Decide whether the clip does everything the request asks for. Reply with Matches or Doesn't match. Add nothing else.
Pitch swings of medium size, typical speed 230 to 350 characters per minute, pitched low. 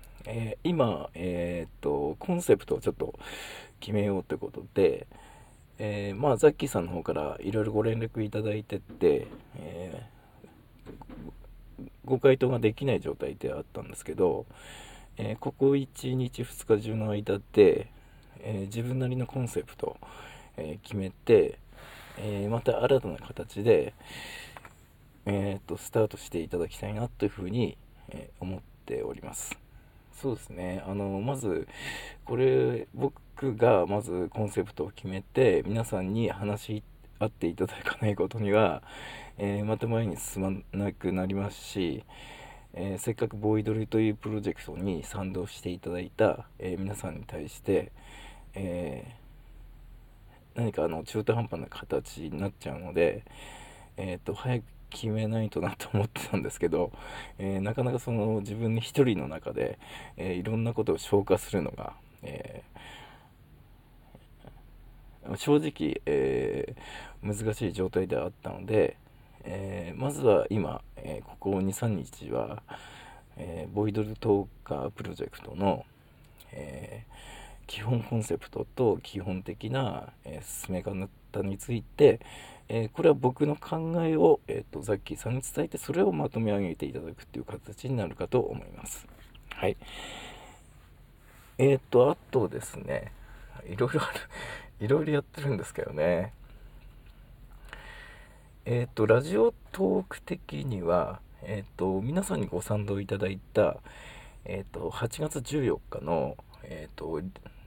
Matches